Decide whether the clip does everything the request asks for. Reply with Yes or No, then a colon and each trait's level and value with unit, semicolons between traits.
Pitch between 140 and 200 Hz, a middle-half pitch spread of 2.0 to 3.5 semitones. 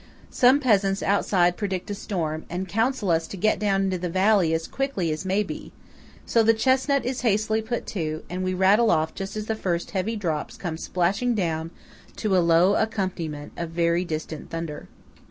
No: high, 190 Hz; average, 4.3 semitones